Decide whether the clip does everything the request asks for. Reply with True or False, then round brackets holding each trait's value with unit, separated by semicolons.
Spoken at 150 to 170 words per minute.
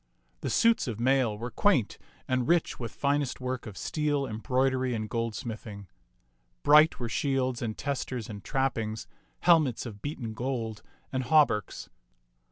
False (140 wpm)